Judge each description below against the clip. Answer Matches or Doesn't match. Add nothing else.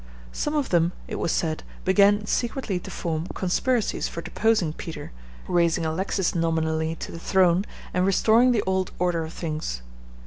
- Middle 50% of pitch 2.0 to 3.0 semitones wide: Doesn't match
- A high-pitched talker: Doesn't match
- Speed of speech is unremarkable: Matches